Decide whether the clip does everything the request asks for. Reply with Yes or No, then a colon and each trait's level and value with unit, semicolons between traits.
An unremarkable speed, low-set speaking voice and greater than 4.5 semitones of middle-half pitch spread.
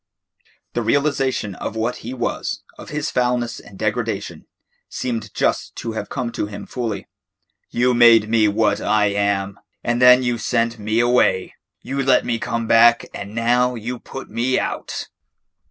No: average, 160 wpm; low, 115 Hz; narrow, 2.5 semitones